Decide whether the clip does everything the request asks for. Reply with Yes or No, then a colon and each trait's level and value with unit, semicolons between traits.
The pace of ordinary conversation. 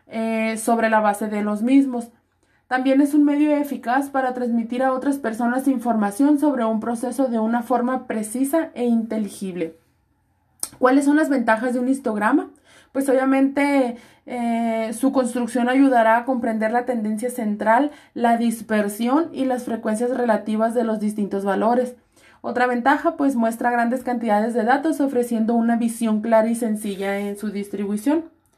Yes: average, 150 wpm